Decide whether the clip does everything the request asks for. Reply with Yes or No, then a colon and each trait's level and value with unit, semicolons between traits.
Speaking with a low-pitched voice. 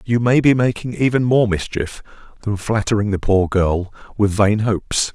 Yes: low, 105 Hz